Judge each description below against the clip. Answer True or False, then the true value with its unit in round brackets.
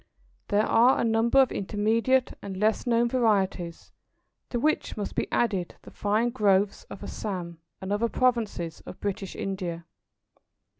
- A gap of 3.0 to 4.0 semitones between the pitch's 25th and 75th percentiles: True (3.5 semitones)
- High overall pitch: True (210 Hz)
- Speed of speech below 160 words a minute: True (145 wpm)